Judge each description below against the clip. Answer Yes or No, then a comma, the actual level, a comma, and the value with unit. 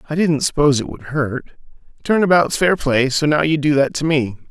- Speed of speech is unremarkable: No, fast, 225 wpm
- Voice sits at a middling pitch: Yes, medium, 150 Hz